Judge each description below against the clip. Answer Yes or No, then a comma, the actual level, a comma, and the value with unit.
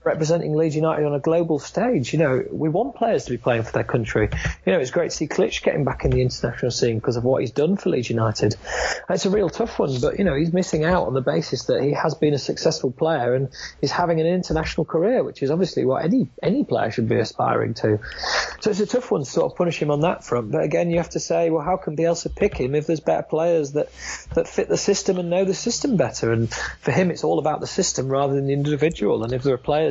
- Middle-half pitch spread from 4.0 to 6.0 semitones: Yes, average, 4.6 semitones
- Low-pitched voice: No, medium, 155 Hz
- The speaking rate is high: Yes, fast, 270 wpm